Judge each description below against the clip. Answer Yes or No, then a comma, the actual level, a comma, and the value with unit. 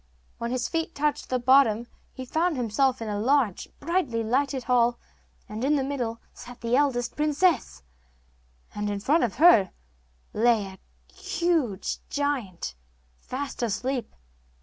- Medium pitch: No, very high, 250 Hz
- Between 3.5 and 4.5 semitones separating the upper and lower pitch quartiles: Yes, average, 4.0 semitones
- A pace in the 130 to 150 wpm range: Yes, average, 140 wpm